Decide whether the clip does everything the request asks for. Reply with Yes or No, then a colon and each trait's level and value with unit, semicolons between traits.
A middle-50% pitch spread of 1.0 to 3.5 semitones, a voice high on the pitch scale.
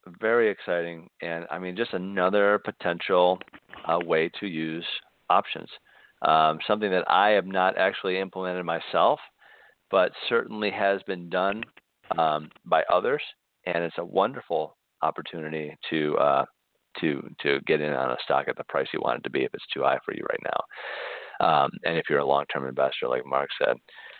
No: average, 3.1 semitones; very low, 85 Hz